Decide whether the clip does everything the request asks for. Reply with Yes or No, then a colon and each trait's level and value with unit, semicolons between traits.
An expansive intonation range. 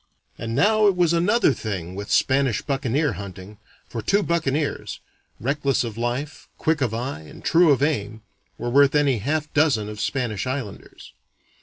Yes: wide, 5.7 semitones